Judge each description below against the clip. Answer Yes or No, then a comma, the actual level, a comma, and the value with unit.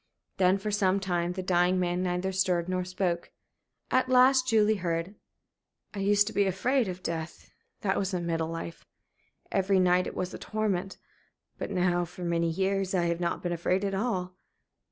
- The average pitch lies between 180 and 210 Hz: Yes, medium, 185 Hz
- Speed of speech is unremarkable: Yes, average, 185 wpm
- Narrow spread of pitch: Yes, narrow, 2.0 semitones